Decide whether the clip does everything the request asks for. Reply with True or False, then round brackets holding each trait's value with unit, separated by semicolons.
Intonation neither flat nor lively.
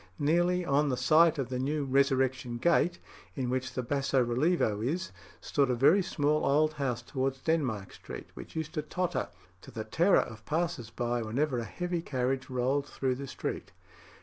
True (3.8 semitones)